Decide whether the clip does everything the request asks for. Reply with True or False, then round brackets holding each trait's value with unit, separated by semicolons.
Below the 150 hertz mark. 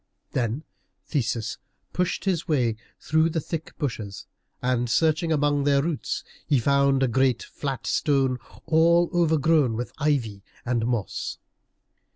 True (140 Hz)